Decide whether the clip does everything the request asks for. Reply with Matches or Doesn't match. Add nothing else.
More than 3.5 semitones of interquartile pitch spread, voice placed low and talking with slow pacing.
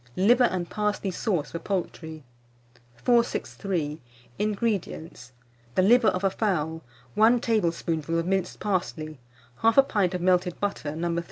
Doesn't match